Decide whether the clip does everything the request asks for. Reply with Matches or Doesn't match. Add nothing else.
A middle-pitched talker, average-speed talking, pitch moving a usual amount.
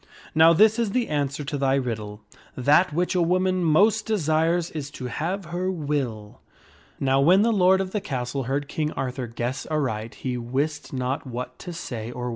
Doesn't match